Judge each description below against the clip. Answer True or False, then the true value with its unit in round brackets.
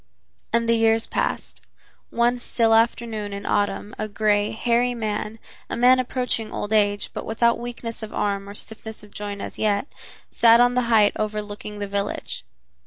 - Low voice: False (220 Hz)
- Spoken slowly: False (170 wpm)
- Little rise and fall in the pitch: True (2.2 semitones)